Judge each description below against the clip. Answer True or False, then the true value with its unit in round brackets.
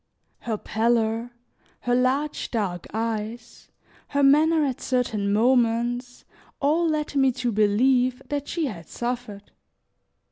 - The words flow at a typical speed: False (115 wpm)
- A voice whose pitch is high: True (245 Hz)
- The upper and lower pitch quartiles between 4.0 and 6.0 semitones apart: False (3.5 semitones)